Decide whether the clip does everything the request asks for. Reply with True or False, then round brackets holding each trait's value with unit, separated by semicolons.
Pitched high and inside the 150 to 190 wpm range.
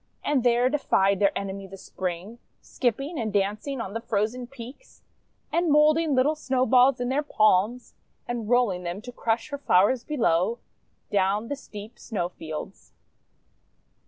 False (235 Hz; 140 wpm)